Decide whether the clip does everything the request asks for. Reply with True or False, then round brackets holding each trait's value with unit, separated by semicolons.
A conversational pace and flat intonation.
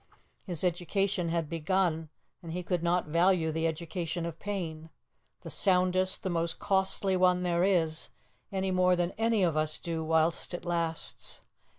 True (160 wpm; 2.2 semitones)